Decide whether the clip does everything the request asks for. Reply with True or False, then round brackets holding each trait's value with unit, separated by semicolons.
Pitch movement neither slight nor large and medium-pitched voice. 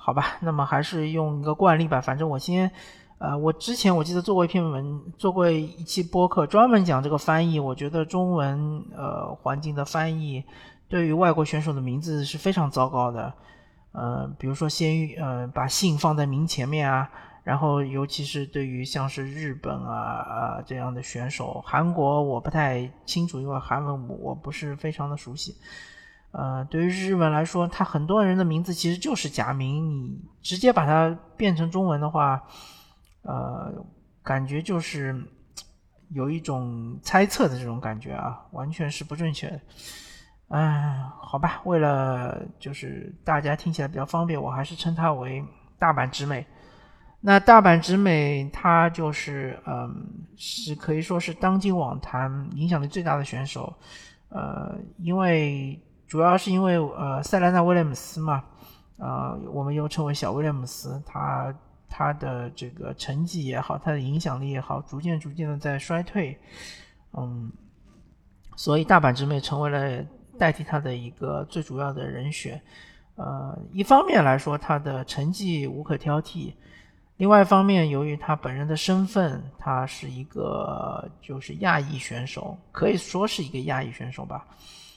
True (4.1 semitones; 150 Hz)